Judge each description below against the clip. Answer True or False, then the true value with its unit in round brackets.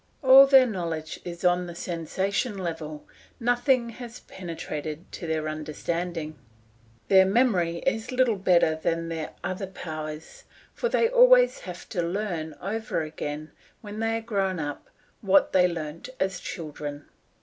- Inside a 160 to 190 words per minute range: False (140 wpm)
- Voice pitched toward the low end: False (180 Hz)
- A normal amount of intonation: False (5.8 semitones)